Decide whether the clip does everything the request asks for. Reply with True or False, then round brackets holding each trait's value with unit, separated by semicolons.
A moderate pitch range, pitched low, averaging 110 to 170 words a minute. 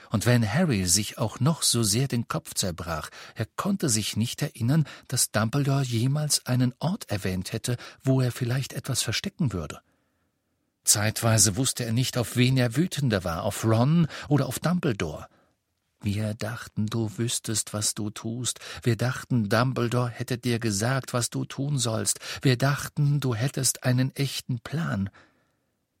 True (3.6 semitones; 125 Hz; 155 wpm)